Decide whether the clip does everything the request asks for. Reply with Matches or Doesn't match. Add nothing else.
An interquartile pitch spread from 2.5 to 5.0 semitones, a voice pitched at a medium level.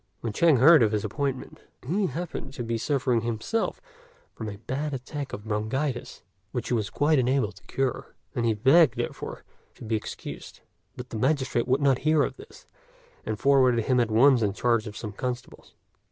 Doesn't match